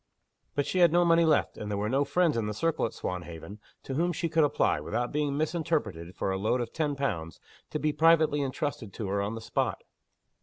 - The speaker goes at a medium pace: No, fast, 225 wpm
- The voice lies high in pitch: No, medium, 140 Hz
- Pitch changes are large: Yes, wide, 7.3 semitones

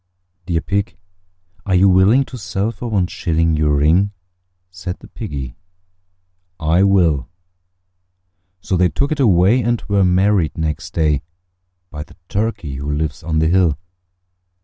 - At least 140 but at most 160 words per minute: Yes, average, 145 wpm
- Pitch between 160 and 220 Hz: No, very low, 90 Hz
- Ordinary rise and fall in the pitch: Yes, average, 4.4 semitones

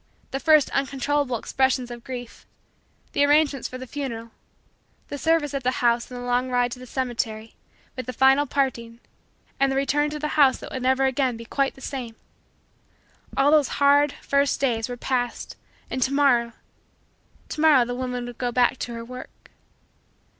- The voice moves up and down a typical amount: No, narrow, 2.3 semitones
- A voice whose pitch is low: No, very high, 260 Hz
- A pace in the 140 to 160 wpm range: No, average, 180 wpm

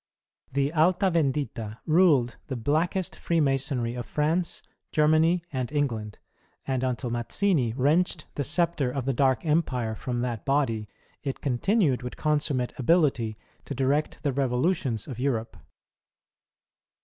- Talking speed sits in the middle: No, slow, 125 wpm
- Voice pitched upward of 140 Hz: No, low, 135 Hz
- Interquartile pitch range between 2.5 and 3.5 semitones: No, average, 4.1 semitones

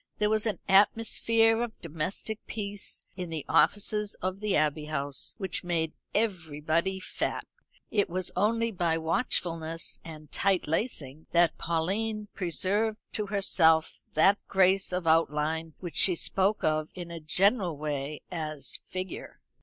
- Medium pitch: Yes, medium, 180 Hz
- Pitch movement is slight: No, average, 4.3 semitones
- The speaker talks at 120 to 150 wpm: Yes, average, 140 wpm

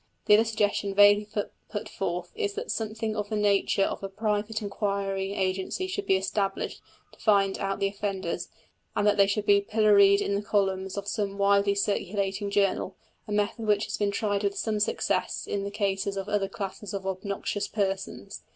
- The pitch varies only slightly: Yes, narrow, 1.1 semitones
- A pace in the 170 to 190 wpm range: Yes, average, 185 wpm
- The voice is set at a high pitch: Yes, high, 200 Hz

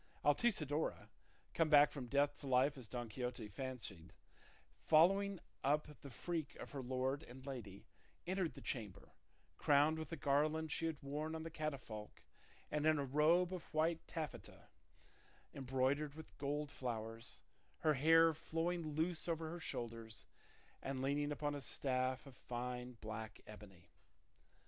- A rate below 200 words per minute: Yes, average, 145 wpm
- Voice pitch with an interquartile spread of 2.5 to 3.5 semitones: No, average, 4.0 semitones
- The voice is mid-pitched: Yes, medium, 145 Hz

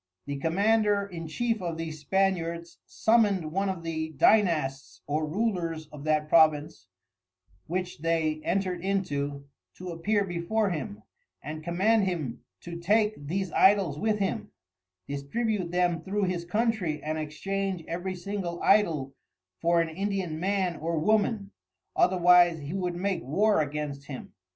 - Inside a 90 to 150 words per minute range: Yes, average, 140 wpm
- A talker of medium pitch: Yes, medium, 175 Hz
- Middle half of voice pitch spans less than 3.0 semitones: No, average, 4.0 semitones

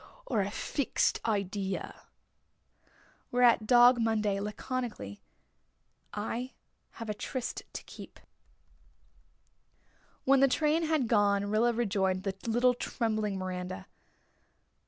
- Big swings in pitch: No, average, 3.6 semitones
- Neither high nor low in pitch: No, high, 215 Hz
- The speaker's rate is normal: No, slow, 100 wpm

